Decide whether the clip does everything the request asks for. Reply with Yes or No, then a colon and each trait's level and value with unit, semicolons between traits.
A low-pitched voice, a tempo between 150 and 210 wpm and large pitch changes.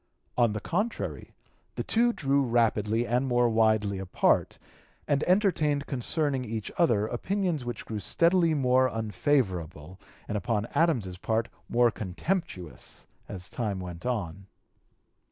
No: low, 120 Hz; slow, 135 wpm; wide, 5.9 semitones